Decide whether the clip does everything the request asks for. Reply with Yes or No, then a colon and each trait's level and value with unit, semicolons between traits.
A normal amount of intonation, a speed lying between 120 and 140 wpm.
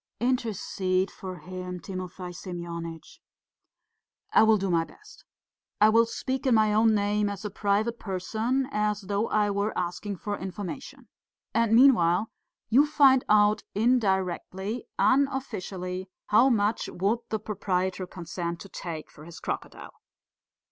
Yes: average, 3.6 semitones; slow, 135 wpm